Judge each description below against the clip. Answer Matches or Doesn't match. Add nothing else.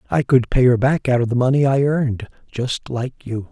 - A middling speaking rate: Doesn't match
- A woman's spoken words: Doesn't match